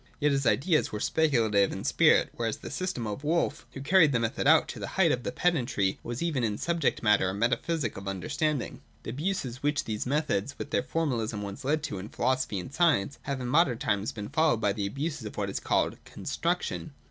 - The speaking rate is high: Yes, fast, 215 wpm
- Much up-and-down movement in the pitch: Yes, wide, 6.3 semitones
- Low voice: Yes, low, 130 Hz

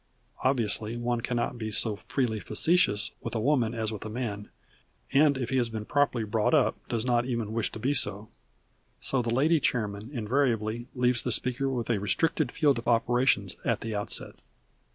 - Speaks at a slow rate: No, average, 190 wpm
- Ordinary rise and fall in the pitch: Yes, average, 3.1 semitones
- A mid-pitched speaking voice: No, low, 120 Hz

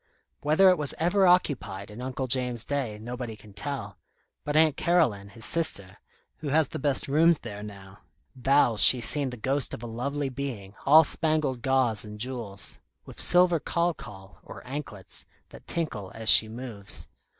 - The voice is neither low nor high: No, low, 130 Hz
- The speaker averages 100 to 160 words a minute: No, average, 170 wpm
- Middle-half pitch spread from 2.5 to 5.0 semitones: No, wide, 5.5 semitones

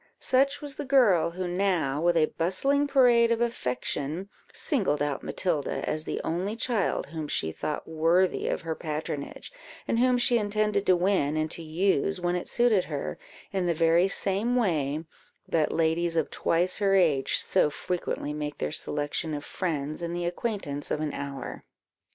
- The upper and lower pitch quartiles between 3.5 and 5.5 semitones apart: Yes, average, 4.8 semitones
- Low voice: No, medium, 175 Hz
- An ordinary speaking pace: Yes, average, 170 wpm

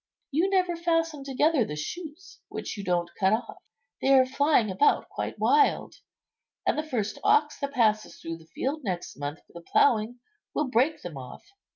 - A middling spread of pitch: No, wide, 8.6 semitones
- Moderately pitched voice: No, very high, 255 Hz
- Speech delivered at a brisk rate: No, average, 180 wpm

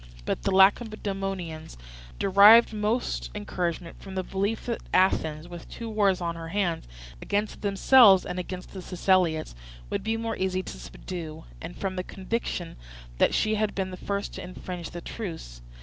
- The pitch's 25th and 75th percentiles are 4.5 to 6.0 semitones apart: No, average, 3.0 semitones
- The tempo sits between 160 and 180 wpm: Yes, average, 165 wpm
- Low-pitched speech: No, high, 190 Hz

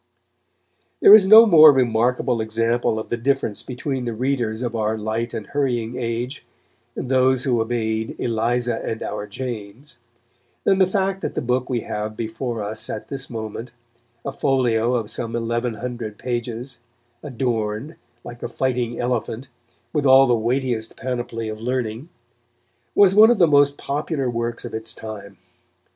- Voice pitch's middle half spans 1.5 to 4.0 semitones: Yes, average, 2.8 semitones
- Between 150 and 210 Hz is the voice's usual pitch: No, low, 120 Hz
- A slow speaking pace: No, average, 155 wpm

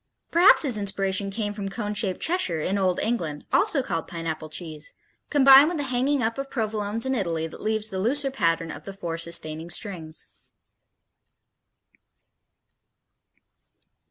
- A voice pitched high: Yes, high, 205 Hz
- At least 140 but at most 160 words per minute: Yes, average, 145 wpm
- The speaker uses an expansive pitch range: Yes, wide, 7.0 semitones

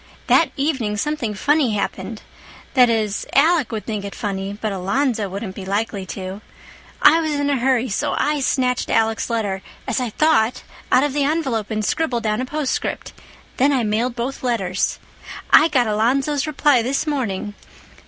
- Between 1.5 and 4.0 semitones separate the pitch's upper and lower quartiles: No, average, 5.0 semitones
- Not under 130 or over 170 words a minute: Yes, average, 165 wpm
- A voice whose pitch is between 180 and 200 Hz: No, high, 235 Hz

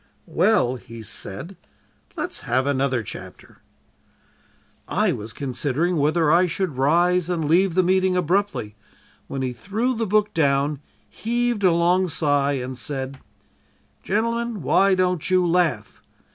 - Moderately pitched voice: Yes, medium, 170 Hz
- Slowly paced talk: Yes, slow, 130 wpm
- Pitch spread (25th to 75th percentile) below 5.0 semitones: No, average, 5.3 semitones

